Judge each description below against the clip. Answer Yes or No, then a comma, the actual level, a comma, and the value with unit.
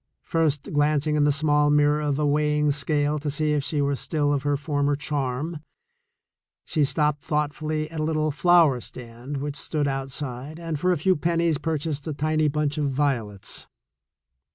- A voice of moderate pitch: Yes, medium, 150 Hz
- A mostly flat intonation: Yes, narrow, 1.4 semitones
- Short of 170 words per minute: No, average, 175 wpm